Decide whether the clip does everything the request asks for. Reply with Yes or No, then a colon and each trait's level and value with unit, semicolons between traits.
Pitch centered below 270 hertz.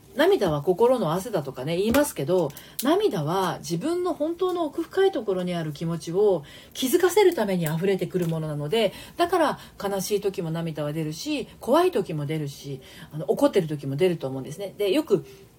Yes: medium, 185 Hz